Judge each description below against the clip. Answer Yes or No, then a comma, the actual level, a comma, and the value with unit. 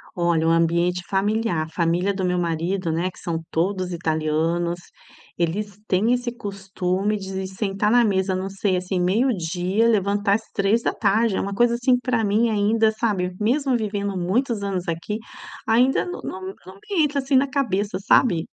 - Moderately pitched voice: No, high, 195 Hz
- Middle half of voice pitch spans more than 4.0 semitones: No, average, 3.7 semitones